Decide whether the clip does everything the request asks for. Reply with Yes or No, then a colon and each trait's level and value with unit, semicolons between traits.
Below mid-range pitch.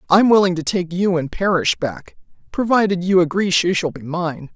No: medium, 180 Hz